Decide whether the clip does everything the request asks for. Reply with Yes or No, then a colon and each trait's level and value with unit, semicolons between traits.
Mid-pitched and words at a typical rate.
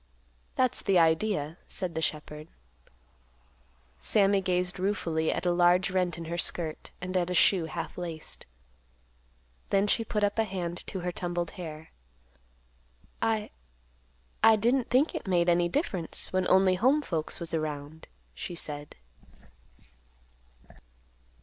No: medium, 175 Hz; slow, 130 wpm